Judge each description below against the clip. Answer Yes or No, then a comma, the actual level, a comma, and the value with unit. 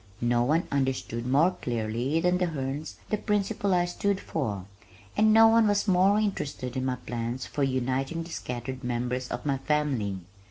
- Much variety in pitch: Yes, wide, 6.4 semitones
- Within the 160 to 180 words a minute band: Yes, average, 170 wpm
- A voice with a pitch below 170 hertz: Yes, low, 135 Hz